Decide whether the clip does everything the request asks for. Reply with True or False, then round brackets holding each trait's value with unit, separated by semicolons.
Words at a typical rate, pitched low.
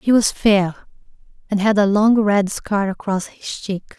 False (180 wpm; 200 Hz)